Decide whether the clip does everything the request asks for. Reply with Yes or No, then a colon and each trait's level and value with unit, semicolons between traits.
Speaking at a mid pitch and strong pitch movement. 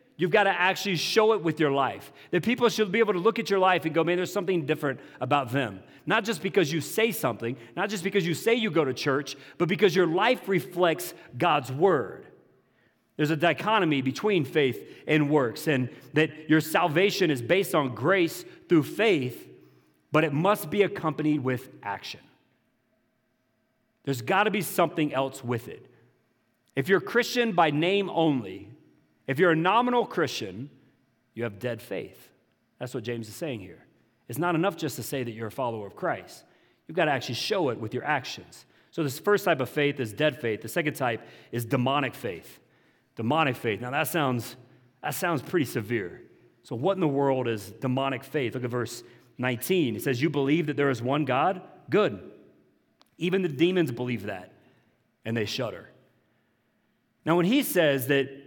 Yes: medium, 150 Hz; wide, 5.9 semitones